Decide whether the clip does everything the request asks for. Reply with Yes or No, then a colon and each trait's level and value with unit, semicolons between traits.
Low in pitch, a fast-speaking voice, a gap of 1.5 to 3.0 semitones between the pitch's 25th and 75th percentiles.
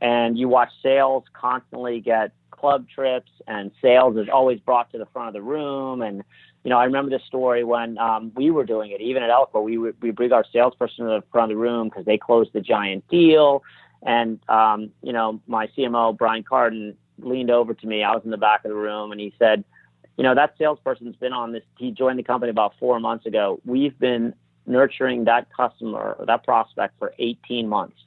Yes: low, 120 Hz; fast, 215 wpm; narrow, 2.4 semitones